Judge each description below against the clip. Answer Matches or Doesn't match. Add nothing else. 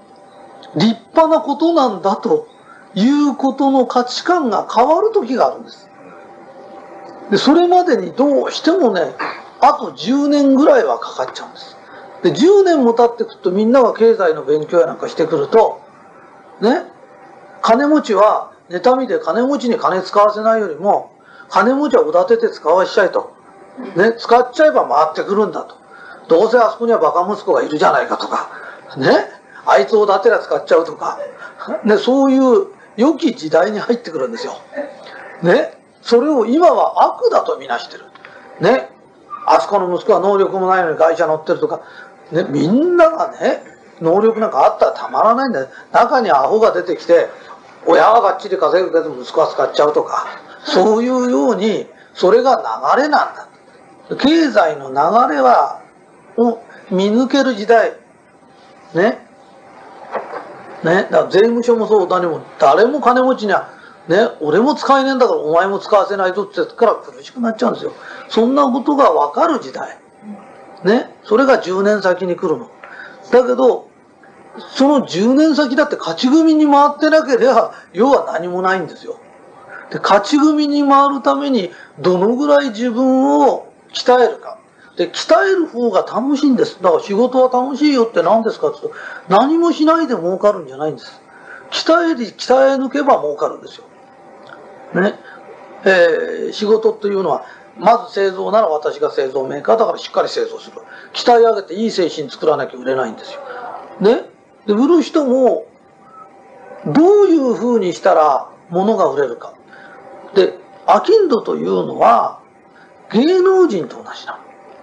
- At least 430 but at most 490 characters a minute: Doesn't match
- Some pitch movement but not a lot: Doesn't match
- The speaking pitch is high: Matches